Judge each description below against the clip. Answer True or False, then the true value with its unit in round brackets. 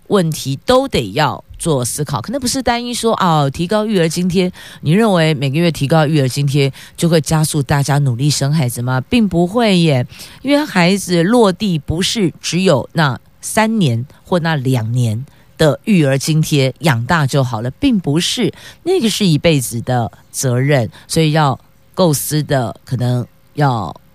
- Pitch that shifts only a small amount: False (5.1 semitones)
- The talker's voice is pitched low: False (155 Hz)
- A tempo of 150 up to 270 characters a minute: True (245 characters per minute)